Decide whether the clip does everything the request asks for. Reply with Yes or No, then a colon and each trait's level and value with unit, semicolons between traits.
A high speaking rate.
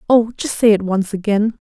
Yes: fast, 215 wpm